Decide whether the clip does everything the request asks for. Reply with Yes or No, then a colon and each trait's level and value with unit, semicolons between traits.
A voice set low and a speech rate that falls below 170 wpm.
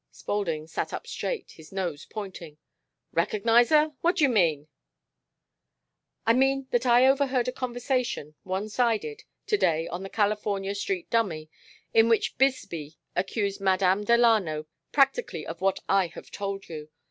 No: high, 210 Hz; average, 145 wpm